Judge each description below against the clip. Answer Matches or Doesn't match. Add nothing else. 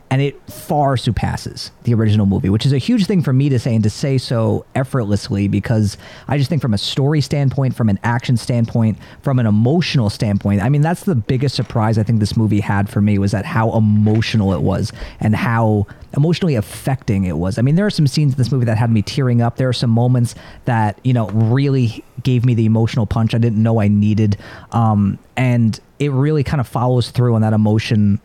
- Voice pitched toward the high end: Doesn't match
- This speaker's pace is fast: Matches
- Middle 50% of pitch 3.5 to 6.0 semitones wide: Matches